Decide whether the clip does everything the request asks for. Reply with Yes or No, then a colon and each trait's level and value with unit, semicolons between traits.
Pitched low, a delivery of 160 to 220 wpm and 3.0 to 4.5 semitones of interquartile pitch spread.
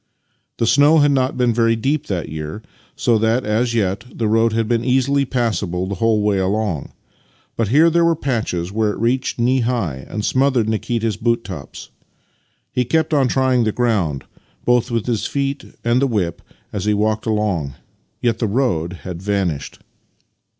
Yes: low, 115 Hz; average, 175 wpm; average, 3.8 semitones